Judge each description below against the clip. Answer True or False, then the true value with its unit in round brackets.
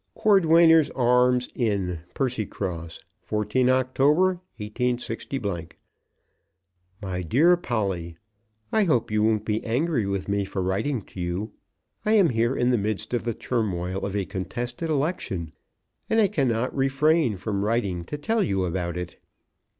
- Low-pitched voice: True (115 Hz)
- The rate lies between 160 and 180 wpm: False (140 wpm)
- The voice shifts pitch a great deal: True (5.8 semitones)